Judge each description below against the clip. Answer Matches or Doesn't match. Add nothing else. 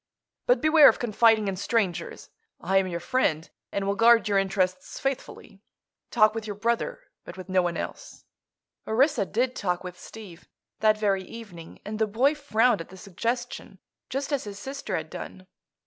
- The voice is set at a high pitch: Matches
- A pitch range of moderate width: Matches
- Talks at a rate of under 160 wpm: Doesn't match